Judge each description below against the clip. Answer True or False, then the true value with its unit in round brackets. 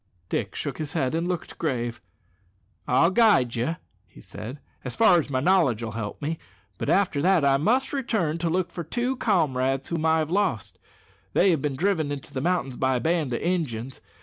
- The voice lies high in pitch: False (155 Hz)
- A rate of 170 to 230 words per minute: True (200 wpm)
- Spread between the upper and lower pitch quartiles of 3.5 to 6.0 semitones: True (5.5 semitones)